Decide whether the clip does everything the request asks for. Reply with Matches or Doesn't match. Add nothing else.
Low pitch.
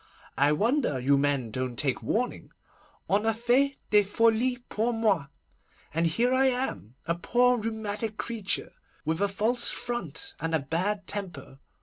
Doesn't match